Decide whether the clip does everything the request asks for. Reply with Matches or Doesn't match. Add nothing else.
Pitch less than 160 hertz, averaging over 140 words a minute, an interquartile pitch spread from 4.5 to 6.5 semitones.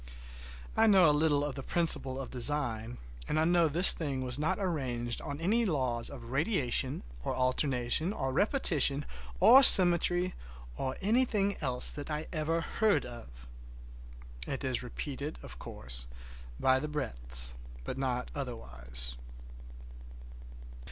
Doesn't match